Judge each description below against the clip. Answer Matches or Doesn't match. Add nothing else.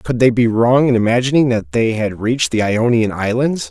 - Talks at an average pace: Doesn't match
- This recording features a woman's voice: Doesn't match